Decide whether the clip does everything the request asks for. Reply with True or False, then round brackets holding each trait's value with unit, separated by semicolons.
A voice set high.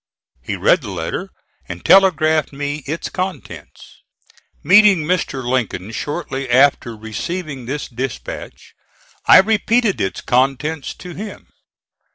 False (145 Hz)